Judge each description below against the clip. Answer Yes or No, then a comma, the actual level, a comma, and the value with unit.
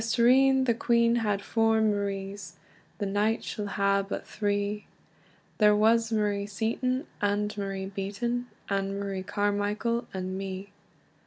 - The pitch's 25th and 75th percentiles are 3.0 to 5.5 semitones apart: No, narrow, 2.4 semitones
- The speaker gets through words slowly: Yes, slow, 130 wpm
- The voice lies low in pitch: No, high, 205 Hz